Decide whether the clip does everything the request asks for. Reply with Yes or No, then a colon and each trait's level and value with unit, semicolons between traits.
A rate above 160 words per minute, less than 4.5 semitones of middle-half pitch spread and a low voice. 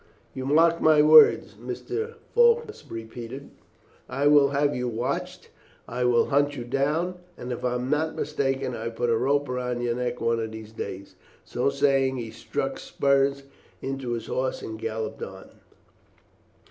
Yes: average, 170 wpm; average, 3.2 semitones; low, 130 Hz